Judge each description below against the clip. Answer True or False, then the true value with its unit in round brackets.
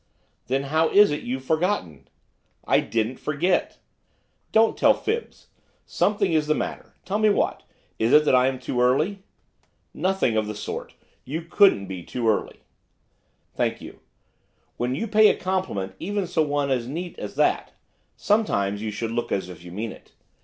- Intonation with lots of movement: True (8.6 semitones)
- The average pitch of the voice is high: False (140 Hz)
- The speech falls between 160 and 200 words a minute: True (175 wpm)